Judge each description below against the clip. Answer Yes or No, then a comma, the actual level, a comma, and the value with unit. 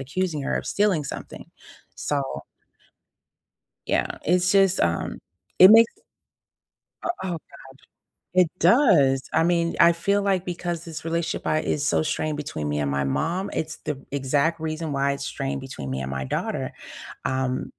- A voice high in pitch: No, medium, 155 Hz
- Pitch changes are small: No, average, 4.6 semitones